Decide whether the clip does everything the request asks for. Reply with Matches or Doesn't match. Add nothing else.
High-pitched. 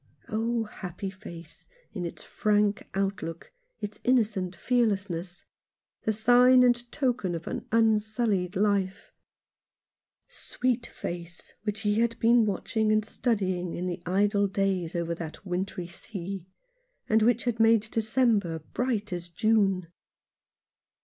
Matches